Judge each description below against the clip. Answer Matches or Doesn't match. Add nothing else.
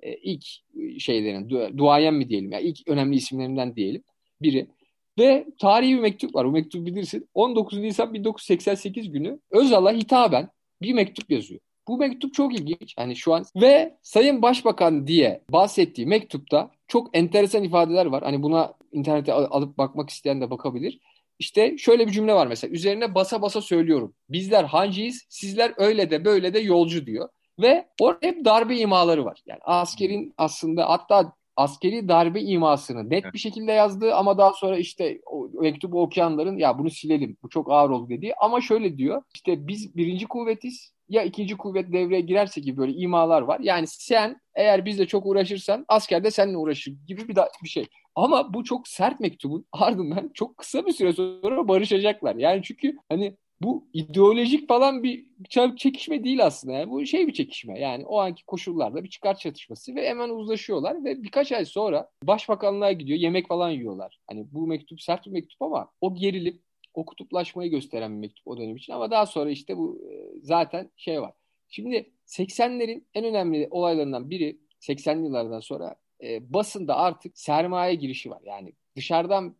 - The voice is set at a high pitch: Matches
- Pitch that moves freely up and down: Matches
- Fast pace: Matches